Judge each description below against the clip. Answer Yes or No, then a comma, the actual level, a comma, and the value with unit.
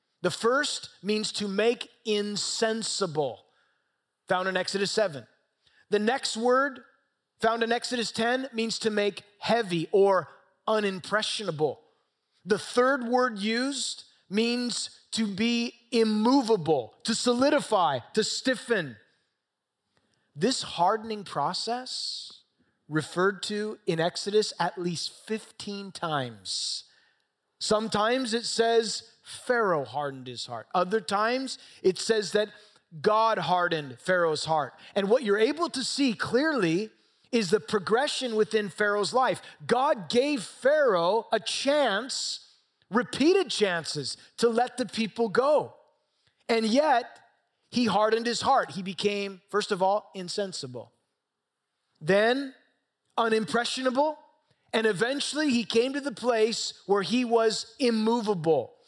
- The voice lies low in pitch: No, high, 220 Hz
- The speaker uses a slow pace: Yes, slow, 115 wpm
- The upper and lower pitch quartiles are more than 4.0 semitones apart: No, average, 3.6 semitones